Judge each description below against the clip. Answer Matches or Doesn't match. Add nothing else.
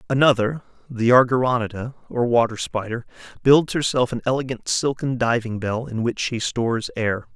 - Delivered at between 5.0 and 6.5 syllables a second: Matches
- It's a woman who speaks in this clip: Doesn't match